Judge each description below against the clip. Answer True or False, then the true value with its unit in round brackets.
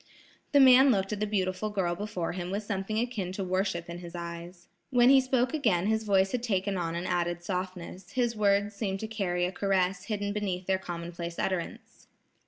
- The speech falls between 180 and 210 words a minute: True (195 wpm)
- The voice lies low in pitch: False (195 Hz)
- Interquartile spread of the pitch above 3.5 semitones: False (3.1 semitones)